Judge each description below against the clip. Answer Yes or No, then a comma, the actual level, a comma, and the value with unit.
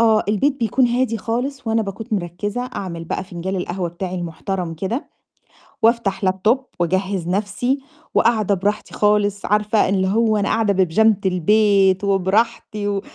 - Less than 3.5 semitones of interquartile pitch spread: Yes, average, 2.9 semitones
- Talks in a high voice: Yes, high, 205 Hz